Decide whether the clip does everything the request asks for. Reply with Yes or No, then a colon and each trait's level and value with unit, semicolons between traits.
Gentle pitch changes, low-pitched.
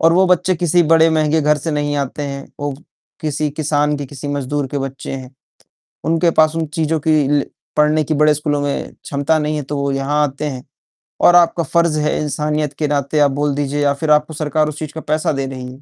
No: narrow, 1.7 semitones; medium, 150 Hz